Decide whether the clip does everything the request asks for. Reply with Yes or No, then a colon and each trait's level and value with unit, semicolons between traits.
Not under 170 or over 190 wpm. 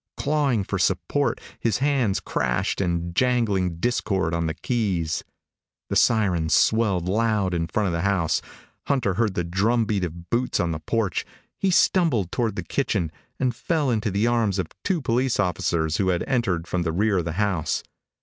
Yes: average, 180 wpm